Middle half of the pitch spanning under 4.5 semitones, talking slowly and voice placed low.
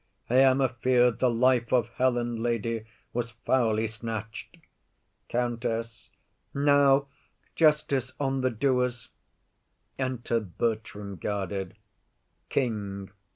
Yes: average, 2.7 semitones; slow, 100 wpm; low, 120 Hz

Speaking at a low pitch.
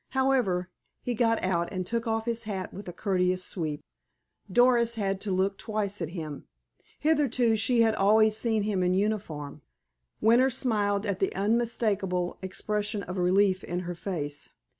No: high, 205 Hz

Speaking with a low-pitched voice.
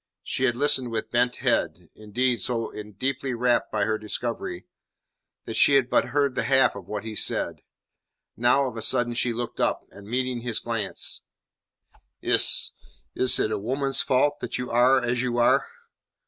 Yes: low, 120 Hz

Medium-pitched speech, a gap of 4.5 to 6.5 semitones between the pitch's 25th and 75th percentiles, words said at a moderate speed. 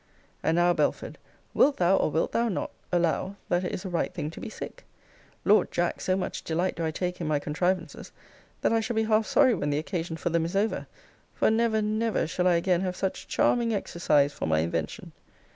No: medium, 180 Hz; average, 4.8 semitones; fast, 215 wpm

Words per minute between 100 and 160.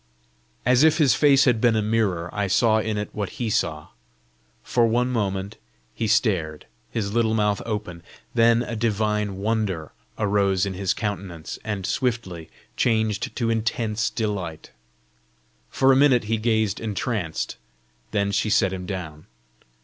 Yes: average, 150 wpm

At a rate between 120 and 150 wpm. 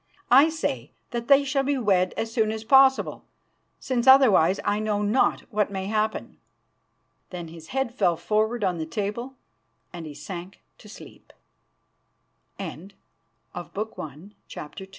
Yes: average, 145 wpm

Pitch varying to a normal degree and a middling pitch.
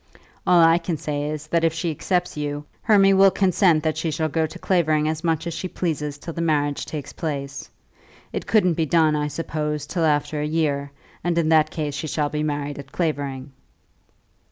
No: narrow, 2.1 semitones; medium, 155 Hz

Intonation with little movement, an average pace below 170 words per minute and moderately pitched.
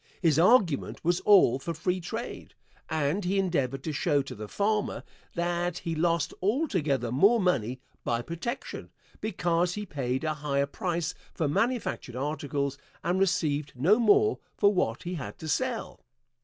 No: wide, 5.4 semitones; average, 155 wpm; medium, 170 Hz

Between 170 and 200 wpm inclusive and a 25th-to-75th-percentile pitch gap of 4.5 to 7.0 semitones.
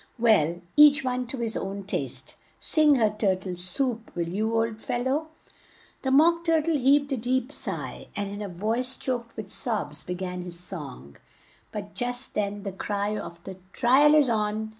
Yes: average, 190 wpm; average, 5.1 semitones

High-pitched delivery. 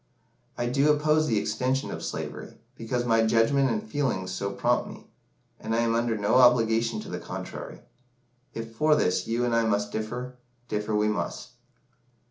No: low, 115 Hz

